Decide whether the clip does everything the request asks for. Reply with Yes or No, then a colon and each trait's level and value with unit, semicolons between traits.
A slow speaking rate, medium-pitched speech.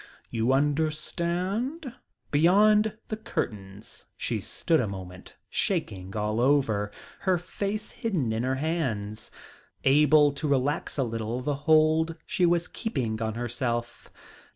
Yes: slow, 125 wpm; medium, 145 Hz